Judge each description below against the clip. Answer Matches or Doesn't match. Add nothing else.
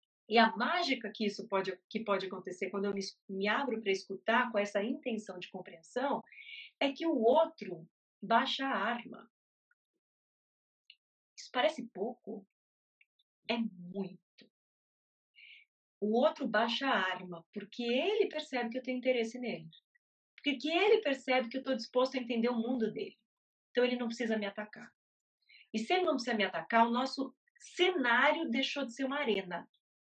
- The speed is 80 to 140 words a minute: Doesn't match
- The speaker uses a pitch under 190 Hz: Doesn't match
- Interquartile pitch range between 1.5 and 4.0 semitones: Doesn't match